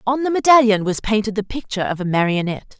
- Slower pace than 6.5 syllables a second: No, 6.7 syllables/s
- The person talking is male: No, female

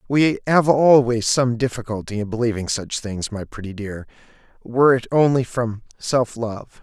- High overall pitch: No, low, 120 Hz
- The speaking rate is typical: Yes, average, 160 wpm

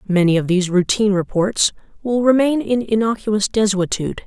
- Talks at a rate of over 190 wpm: No, average, 140 wpm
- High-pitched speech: Yes, high, 205 Hz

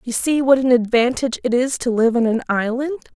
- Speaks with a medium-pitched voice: No, very high, 250 Hz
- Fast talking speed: Yes, fast, 225 wpm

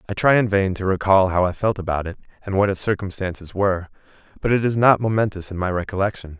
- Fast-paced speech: Yes, fast, 225 wpm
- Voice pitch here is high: No, very low, 95 Hz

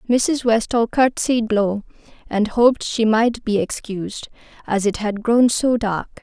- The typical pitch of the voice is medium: No, high, 225 Hz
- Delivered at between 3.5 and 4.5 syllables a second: Yes, 4.0 syllables/s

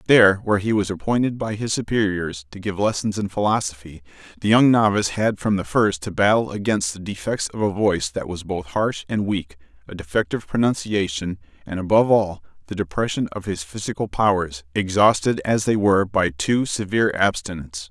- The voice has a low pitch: Yes, low, 100 Hz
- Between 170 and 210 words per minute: Yes, average, 180 wpm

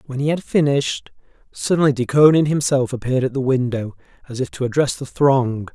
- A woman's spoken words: No, male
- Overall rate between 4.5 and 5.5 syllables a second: No, 5.8 syllables/s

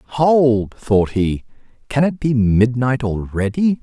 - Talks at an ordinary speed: No, slow, 125 wpm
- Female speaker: No, male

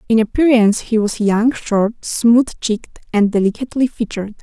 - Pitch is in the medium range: No, high, 225 Hz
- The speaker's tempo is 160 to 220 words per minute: No, average, 150 wpm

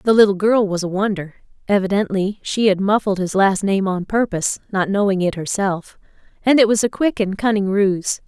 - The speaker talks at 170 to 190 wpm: Yes, average, 180 wpm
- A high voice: Yes, high, 200 Hz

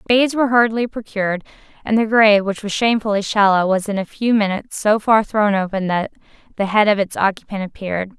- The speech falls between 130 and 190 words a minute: No, average, 200 wpm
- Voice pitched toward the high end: Yes, high, 210 Hz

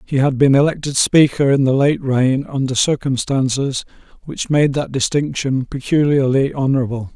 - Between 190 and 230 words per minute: No, average, 140 wpm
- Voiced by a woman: No, male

